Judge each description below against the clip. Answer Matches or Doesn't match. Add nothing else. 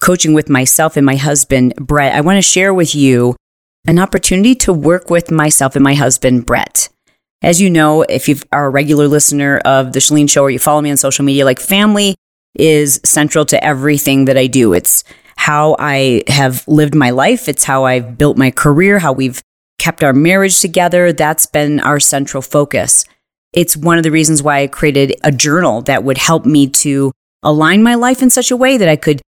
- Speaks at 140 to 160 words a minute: Doesn't match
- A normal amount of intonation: Matches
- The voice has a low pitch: Doesn't match